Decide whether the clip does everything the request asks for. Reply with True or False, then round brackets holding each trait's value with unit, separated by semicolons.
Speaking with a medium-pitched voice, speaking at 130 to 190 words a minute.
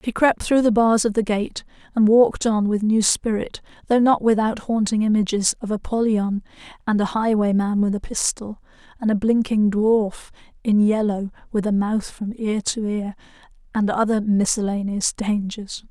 False (215 Hz; 165 wpm)